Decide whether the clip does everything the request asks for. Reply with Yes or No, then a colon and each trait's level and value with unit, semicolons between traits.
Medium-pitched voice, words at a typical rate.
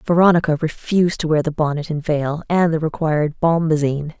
Yes: medium, 155 Hz; average, 170 wpm